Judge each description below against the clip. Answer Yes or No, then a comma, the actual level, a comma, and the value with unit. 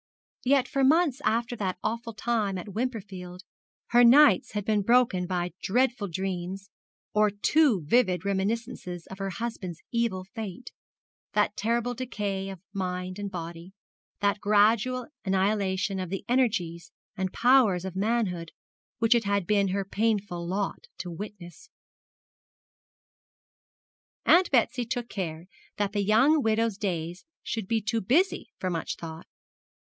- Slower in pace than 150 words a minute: Yes, slow, 135 wpm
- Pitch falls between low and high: No, high, 205 Hz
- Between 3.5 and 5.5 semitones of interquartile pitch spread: Yes, average, 3.9 semitones